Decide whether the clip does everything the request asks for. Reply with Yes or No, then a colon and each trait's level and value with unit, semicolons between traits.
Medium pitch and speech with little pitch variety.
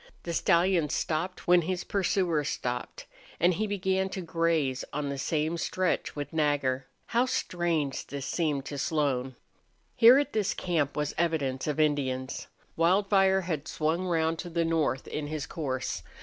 No: medium, 160 Hz; average, 3.8 semitones